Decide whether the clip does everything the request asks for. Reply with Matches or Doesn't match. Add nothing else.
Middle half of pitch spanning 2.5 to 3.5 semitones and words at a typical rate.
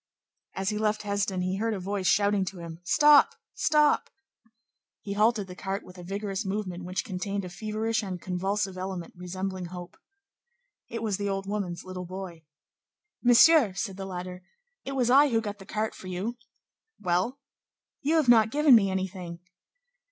Matches